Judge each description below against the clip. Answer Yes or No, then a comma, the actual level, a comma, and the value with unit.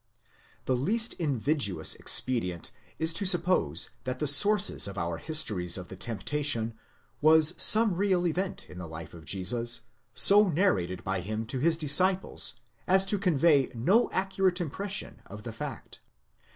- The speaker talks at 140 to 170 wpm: Yes, average, 150 wpm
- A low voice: No, medium, 145 Hz